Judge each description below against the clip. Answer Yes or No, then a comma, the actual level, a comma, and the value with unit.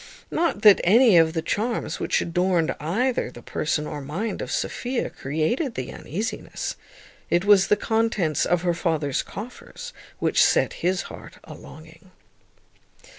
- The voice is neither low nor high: Yes, medium, 180 Hz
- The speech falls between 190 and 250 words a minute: No, average, 145 wpm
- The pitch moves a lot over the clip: Yes, wide, 5.7 semitones